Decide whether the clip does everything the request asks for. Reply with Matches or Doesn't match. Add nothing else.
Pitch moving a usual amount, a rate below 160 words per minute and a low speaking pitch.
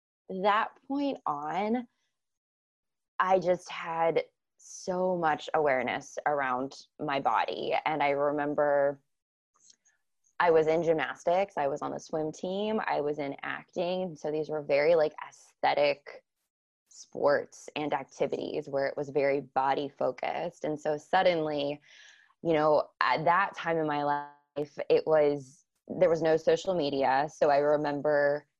Doesn't match